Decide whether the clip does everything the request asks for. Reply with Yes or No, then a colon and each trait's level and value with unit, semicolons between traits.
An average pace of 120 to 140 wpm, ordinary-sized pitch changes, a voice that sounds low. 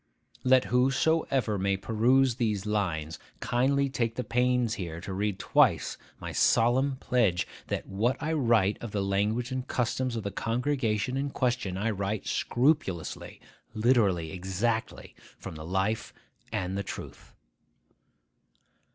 Yes: slow, 135 wpm; average, 4.4 semitones; low, 115 Hz